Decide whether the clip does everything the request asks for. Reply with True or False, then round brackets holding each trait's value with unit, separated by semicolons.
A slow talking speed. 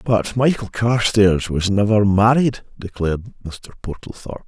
True (105 wpm)